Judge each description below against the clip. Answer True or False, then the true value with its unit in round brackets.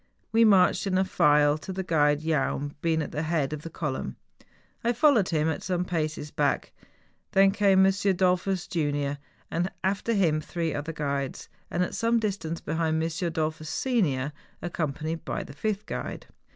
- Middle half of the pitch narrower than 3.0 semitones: False (4.1 semitones)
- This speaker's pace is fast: False (165 wpm)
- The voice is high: False (165 Hz)